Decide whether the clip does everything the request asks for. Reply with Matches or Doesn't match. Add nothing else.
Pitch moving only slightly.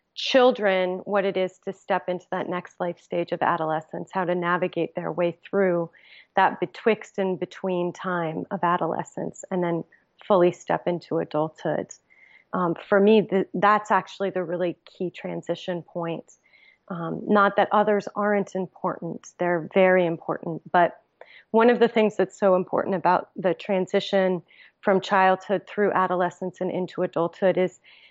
Matches